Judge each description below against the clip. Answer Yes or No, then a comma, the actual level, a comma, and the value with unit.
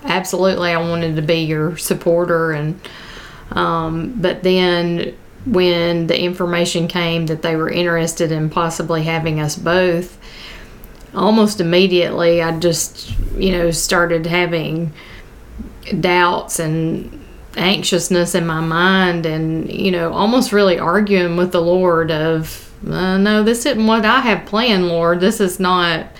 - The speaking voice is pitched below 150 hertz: No, medium, 175 Hz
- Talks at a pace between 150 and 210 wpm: No, slow, 135 wpm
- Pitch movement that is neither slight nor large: No, narrow, 2.0 semitones